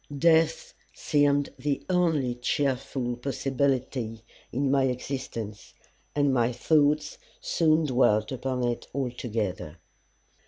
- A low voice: Yes, low, 130 Hz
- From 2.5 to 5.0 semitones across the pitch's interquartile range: Yes, average, 3.0 semitones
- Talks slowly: Yes, slow, 95 wpm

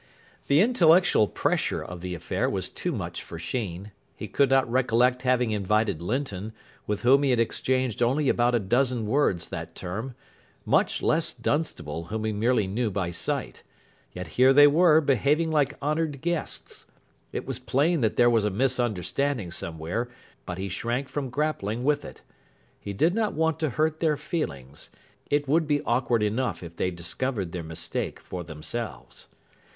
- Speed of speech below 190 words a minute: Yes, average, 165 wpm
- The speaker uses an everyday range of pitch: No, wide, 6.4 semitones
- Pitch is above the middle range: No, low, 120 Hz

